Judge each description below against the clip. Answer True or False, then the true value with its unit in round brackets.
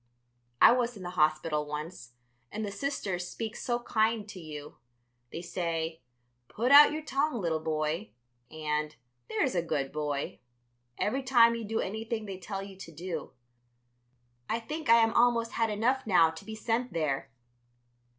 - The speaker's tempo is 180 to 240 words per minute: False (160 wpm)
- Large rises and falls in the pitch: True (6.3 semitones)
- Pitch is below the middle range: False (195 Hz)